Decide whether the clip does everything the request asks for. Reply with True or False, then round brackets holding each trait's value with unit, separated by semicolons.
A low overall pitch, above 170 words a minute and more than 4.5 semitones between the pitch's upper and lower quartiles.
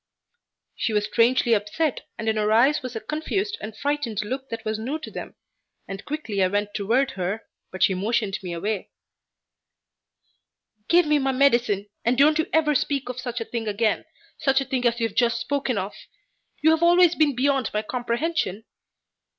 False (240 Hz; 185 wpm; 5.0 semitones)